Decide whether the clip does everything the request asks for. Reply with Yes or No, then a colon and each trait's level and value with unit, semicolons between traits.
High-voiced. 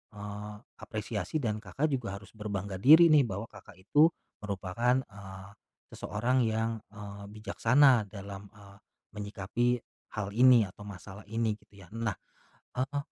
No: low, 105 Hz